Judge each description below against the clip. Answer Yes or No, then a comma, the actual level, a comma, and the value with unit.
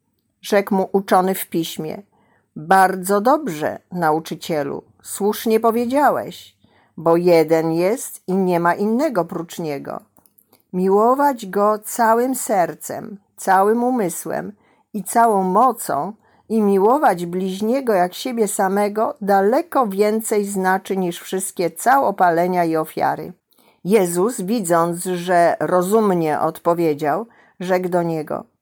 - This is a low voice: No, high, 195 Hz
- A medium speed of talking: No, slow, 105 wpm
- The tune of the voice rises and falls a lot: No, average, 4.1 semitones